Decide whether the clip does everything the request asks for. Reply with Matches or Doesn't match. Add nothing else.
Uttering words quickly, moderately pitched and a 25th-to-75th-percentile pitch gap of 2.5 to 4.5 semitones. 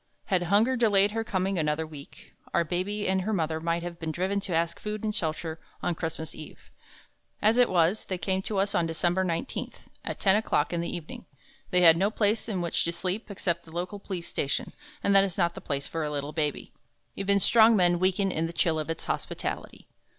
Matches